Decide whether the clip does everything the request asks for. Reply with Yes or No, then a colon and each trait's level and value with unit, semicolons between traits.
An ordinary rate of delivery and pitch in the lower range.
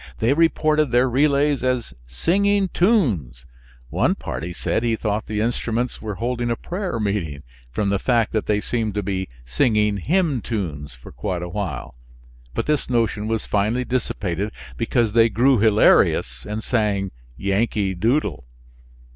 Yes: average, 150 wpm; low, 110 Hz